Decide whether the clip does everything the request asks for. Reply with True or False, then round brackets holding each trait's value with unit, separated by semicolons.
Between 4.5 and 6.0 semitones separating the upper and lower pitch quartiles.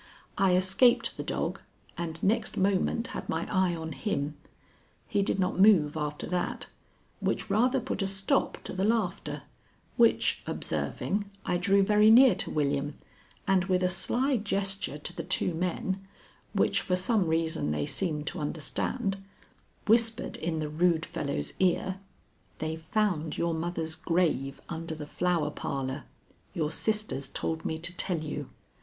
False (3.8 semitones)